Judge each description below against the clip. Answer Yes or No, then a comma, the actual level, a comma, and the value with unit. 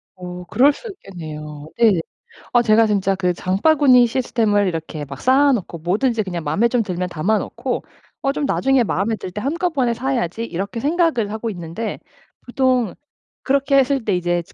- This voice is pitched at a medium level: No, high, 220 Hz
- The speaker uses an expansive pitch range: Yes, wide, 6.4 semitones